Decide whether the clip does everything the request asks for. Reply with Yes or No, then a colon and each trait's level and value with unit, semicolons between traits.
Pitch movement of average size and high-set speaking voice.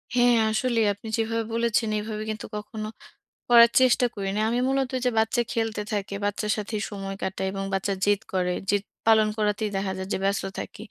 No: narrow, 2.3 semitones; high, 215 Hz